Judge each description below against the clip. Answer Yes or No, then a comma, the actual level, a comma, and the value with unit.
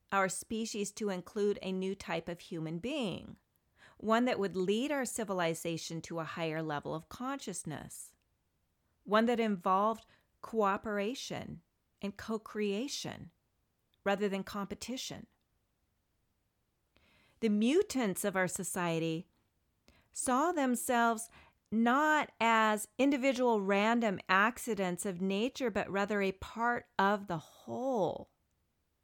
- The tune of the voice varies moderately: Yes, average, 4.7 semitones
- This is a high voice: Yes, high, 200 Hz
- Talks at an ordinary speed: No, slow, 110 wpm